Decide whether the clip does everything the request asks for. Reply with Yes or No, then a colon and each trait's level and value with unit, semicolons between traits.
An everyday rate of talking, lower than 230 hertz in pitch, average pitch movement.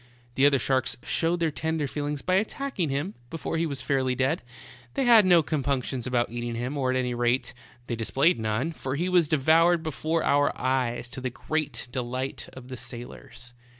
Yes: average, 185 wpm; medium, 140 Hz; average, 4.2 semitones